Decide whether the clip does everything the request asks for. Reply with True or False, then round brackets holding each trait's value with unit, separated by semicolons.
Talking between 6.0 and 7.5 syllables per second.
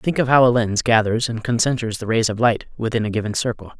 True (6.1 syllables/s)